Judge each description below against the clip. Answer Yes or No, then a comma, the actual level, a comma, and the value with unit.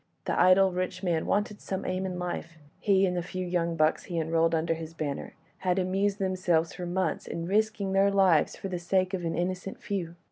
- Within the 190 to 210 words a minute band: Yes, fast, 205 wpm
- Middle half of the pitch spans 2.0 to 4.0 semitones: Yes, narrow, 2.4 semitones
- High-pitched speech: No, medium, 180 Hz